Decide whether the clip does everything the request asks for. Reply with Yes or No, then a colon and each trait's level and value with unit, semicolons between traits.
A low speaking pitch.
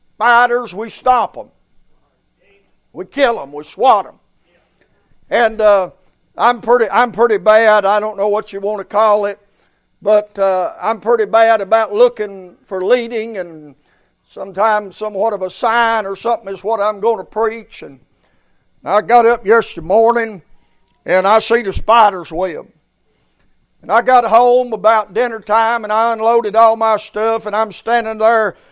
No: high, 220 Hz